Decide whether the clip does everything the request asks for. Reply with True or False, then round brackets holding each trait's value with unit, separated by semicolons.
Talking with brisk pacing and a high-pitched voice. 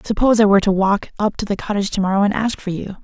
True (275 wpm; 205 Hz)